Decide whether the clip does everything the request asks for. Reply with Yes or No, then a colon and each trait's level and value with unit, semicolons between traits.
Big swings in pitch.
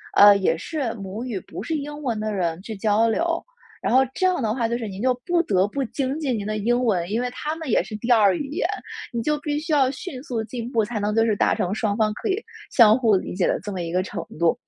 No: average, 4.6 semitones